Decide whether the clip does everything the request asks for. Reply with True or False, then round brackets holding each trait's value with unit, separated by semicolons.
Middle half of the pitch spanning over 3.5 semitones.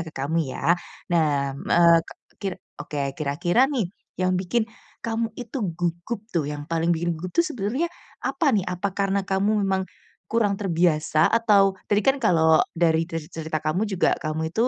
True (4.3 semitones)